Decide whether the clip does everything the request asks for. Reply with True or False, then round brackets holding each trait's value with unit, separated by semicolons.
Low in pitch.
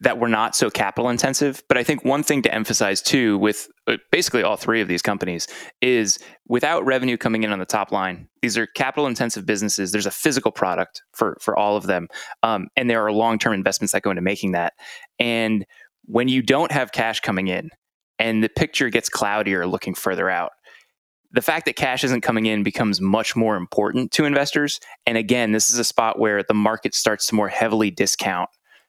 True (110 Hz)